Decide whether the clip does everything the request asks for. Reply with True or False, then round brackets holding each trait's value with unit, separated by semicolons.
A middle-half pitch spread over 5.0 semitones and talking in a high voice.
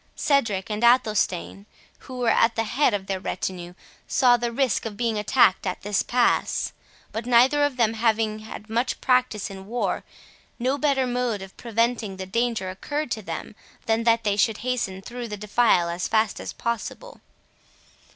False (3.3 semitones; 225 Hz)